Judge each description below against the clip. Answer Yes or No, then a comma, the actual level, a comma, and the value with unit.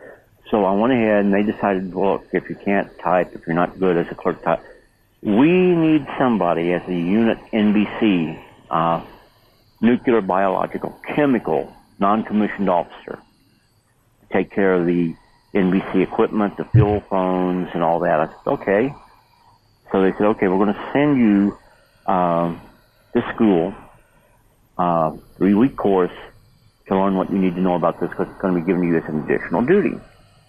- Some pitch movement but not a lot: Yes, average, 3.1 semitones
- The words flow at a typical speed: Yes, average, 170 wpm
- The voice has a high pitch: No, very low, 95 Hz